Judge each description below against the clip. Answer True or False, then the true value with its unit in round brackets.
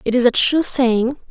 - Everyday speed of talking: False (230 wpm)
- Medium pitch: False (255 Hz)